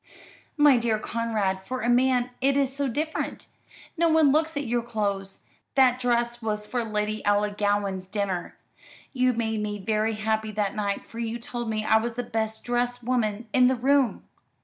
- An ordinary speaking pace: Yes, average, 175 wpm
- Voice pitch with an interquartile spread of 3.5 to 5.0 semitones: No, average, 3.0 semitones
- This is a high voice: Yes, high, 230 Hz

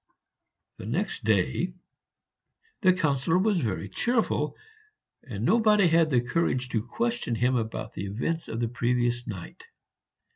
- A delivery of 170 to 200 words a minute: No, slow, 135 wpm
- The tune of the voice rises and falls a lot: Yes, wide, 7.8 semitones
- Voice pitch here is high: No, low, 125 Hz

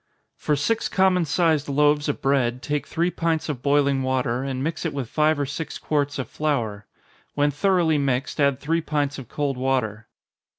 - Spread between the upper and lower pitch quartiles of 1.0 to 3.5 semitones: Yes, narrow, 2.6 semitones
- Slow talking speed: No, average, 185 wpm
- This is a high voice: No, medium, 145 Hz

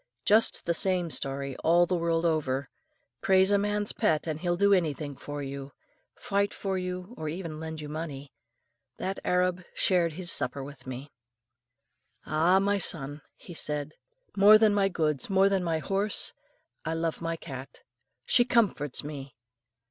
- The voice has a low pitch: No, medium, 165 Hz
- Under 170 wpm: Yes, average, 160 wpm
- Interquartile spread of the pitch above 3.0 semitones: Yes, average, 4.6 semitones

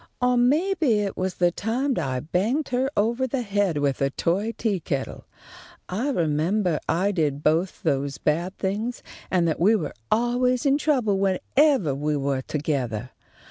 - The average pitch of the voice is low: No, high, 190 Hz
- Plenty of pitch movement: Yes, wide, 8.2 semitones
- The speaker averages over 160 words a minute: No, average, 155 wpm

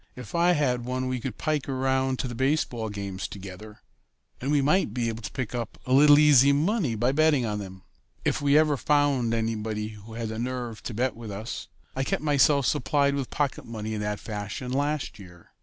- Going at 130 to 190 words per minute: No, fast, 205 wpm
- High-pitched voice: No, low, 125 Hz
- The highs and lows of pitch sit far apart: No, average, 4.4 semitones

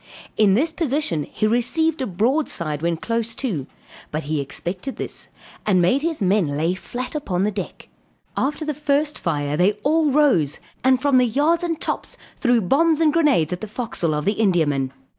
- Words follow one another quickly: No, average, 180 wpm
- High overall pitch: Yes, high, 225 Hz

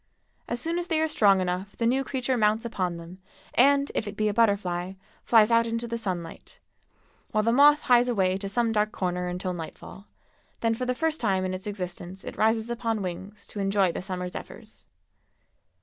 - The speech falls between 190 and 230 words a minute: Yes, average, 195 wpm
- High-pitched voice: Yes, high, 215 Hz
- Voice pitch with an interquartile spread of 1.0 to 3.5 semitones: No, average, 4.2 semitones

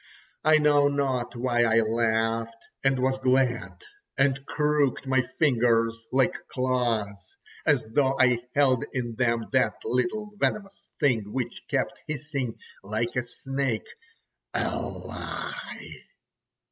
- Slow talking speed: Yes, slow, 120 wpm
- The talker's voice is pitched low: Yes, low, 130 Hz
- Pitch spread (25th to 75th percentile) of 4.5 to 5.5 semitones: No, average, 3.1 semitones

